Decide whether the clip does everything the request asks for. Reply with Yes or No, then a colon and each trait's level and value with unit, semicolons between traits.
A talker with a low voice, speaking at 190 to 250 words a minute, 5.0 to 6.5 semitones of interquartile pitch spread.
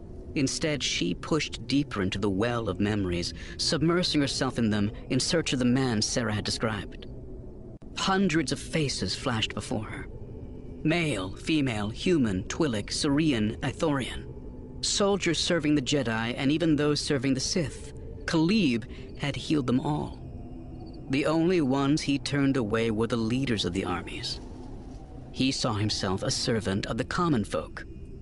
No: low, 130 Hz; average, 145 wpm; wide, 5.6 semitones